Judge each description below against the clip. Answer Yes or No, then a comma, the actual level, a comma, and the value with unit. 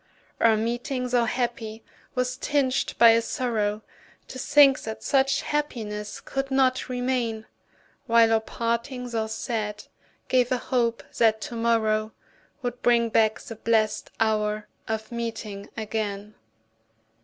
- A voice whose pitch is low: No, high, 230 Hz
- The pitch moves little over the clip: Yes, narrow, 2.3 semitones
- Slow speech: Yes, slow, 130 wpm